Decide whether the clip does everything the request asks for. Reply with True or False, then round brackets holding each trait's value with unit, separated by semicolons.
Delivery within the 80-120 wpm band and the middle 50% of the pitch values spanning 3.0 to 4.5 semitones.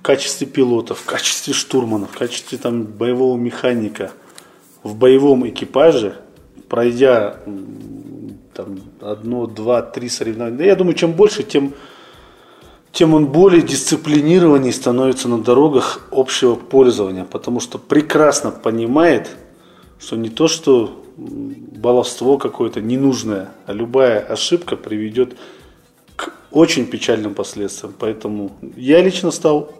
False (115 wpm; 4.9 semitones)